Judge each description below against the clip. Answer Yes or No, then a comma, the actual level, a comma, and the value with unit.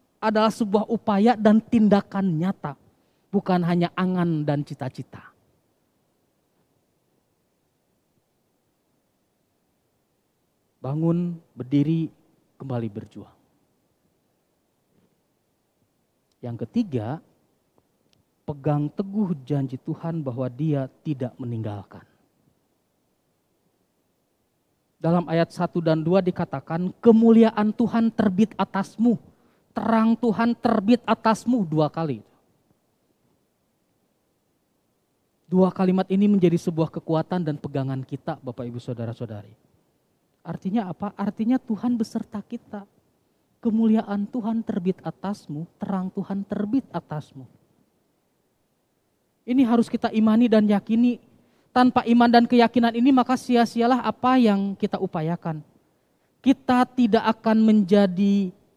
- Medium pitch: No, high, 195 Hz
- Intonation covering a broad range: Yes, wide, 6.5 semitones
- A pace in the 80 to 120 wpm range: Yes, average, 90 wpm